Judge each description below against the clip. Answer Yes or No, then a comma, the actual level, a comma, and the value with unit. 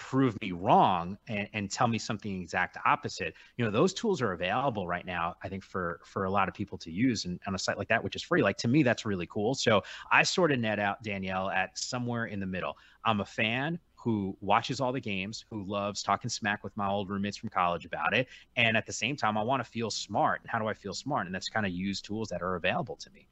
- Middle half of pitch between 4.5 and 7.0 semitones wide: No, average, 3.0 semitones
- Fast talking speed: Yes, fast, 265 wpm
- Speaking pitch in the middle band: No, low, 105 Hz